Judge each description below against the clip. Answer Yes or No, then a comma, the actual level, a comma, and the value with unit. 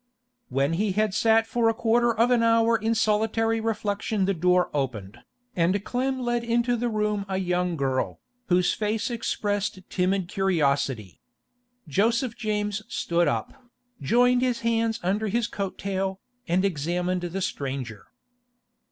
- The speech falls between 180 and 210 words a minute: No, average, 145 wpm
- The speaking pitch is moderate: No, high, 205 Hz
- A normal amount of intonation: Yes, average, 4.2 semitones